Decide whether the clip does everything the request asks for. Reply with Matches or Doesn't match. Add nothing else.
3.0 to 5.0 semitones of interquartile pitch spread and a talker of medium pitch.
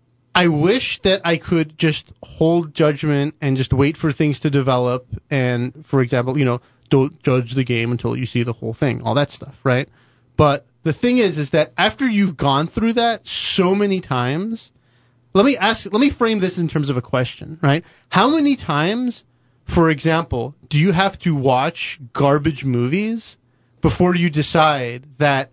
Doesn't match